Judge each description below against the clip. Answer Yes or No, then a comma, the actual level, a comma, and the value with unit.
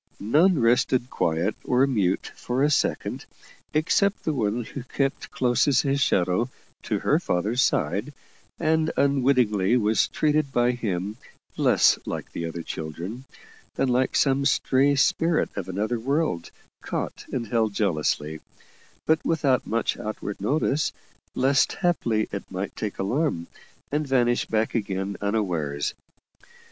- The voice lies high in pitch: No, low, 120 Hz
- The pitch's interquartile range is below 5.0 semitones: No, wide, 5.6 semitones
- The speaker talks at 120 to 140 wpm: Yes, slow, 135 wpm